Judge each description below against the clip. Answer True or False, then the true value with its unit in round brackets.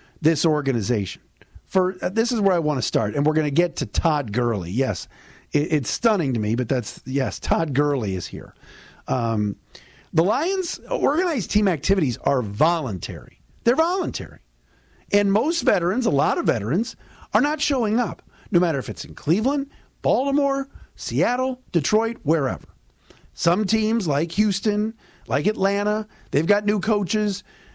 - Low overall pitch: False (175 Hz)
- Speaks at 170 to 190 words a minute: False (155 wpm)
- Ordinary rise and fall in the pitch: False (8.2 semitones)